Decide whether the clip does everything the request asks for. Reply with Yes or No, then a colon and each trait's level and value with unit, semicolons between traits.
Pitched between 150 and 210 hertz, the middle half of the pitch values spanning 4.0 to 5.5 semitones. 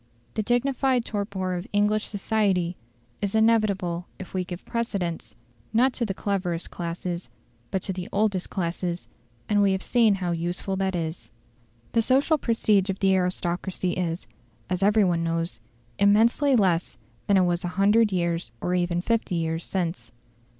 No: high, 190 Hz; average, 3.3 semitones